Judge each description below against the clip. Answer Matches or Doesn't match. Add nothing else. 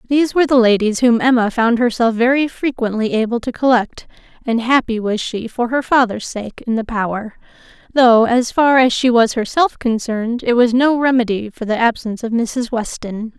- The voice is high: Matches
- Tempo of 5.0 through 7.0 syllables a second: Matches